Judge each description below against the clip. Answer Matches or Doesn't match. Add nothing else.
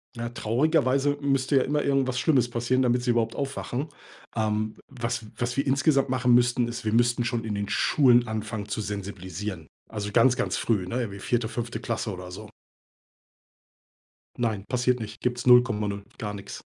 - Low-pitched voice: Matches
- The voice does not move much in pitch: Doesn't match